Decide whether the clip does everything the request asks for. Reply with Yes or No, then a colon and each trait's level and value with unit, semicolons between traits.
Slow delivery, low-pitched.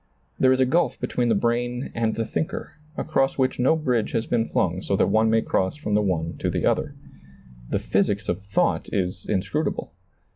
No: average, 195 wpm; low, 115 Hz